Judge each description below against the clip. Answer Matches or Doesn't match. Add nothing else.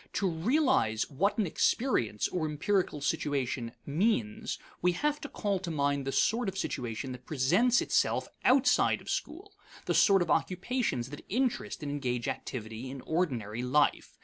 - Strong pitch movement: Matches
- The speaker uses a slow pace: Doesn't match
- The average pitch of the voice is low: Doesn't match